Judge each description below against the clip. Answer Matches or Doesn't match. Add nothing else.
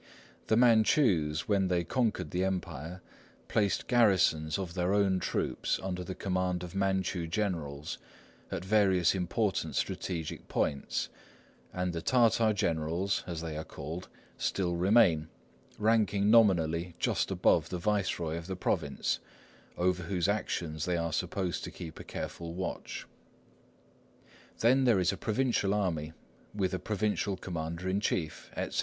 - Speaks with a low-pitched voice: Matches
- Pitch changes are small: Doesn't match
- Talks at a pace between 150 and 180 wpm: Doesn't match